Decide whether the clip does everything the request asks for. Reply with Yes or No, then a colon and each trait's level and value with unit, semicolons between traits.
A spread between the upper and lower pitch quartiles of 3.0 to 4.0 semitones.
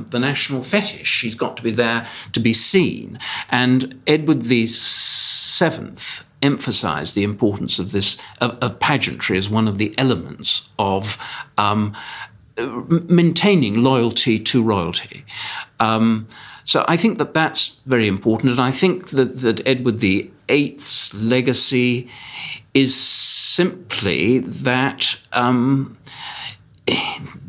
Yes: average, 3.5 semitones